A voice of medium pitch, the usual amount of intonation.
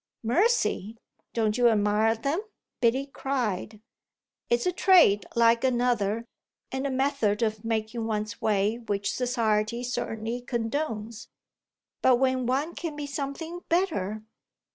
No: high, 235 Hz; average, 3.9 semitones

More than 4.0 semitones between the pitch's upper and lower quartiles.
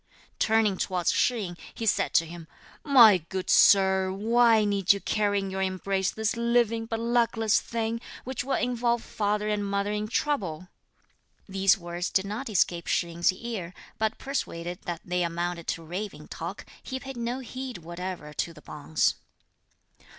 Yes: average, 4.4 semitones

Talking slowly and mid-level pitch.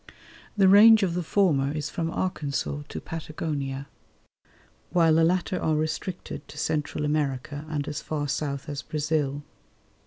No: average, 145 wpm; medium, 155 Hz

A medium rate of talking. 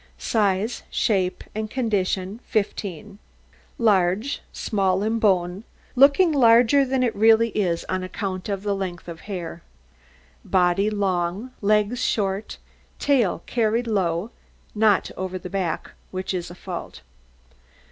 No: slow, 125 wpm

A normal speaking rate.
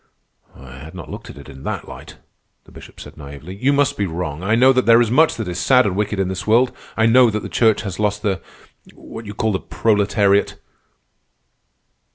No: fast, 210 wpm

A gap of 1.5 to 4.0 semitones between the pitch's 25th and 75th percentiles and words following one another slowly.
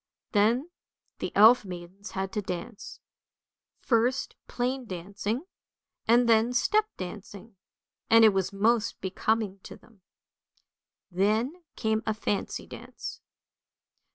Yes: average, 3.2 semitones; slow, 110 wpm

